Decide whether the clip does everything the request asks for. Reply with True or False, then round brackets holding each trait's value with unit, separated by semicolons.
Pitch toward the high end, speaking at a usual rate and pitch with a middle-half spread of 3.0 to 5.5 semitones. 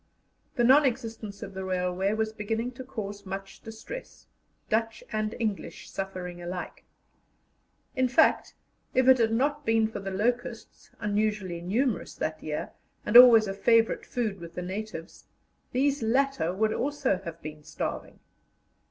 True (215 Hz; 145 wpm; 4.1 semitones)